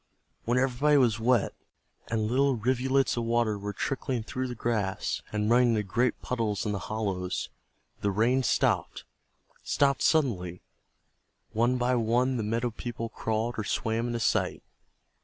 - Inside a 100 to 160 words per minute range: Yes, average, 150 wpm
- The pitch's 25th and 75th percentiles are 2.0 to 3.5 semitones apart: Yes, average, 2.8 semitones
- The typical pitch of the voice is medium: No, low, 115 Hz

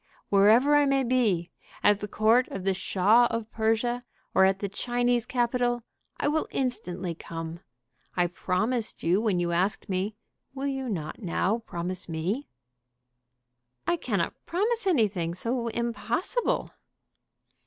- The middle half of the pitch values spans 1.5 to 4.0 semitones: No, average, 5.0 semitones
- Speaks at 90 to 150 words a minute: Yes, slow, 135 wpm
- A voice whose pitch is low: No, high, 220 Hz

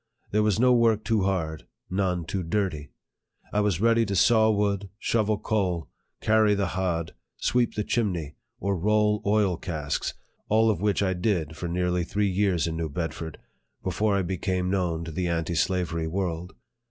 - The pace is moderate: Yes, average, 170 wpm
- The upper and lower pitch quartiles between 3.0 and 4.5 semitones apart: Yes, average, 3.8 semitones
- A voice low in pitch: Yes, very low, 95 Hz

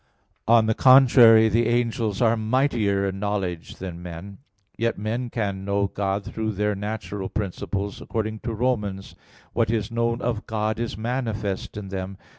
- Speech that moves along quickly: No, average, 160 wpm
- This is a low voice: Yes, low, 110 Hz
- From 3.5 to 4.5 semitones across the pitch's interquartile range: No, average, 2.8 semitones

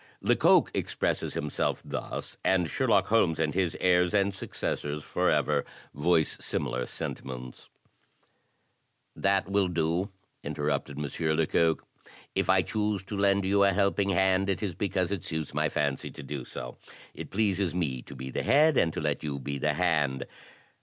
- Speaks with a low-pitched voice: Yes, very low, 90 Hz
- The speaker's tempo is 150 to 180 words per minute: Yes, average, 160 wpm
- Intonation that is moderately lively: Yes, average, 4.9 semitones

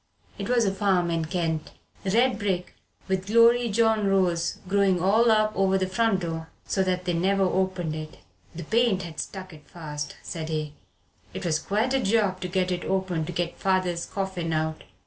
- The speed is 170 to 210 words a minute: Yes, average, 185 wpm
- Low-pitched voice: No, medium, 185 Hz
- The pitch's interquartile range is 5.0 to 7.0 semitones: No, average, 3.0 semitones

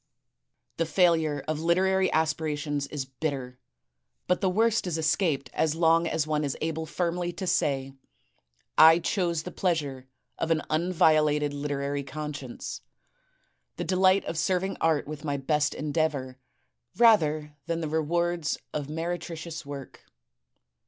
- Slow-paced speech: Yes, slow, 130 wpm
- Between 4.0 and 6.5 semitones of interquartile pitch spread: No, average, 2.7 semitones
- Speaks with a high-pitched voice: No, medium, 155 Hz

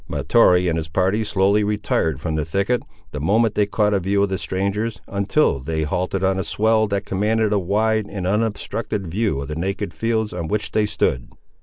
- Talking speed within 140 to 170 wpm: No, average, 200 wpm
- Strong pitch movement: No, average, 2.9 semitones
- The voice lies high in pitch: No, low, 100 Hz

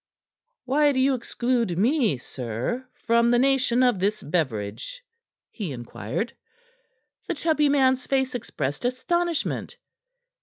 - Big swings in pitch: Yes, wide, 7.0 semitones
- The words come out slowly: Yes, slow, 115 wpm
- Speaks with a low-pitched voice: No, high, 245 Hz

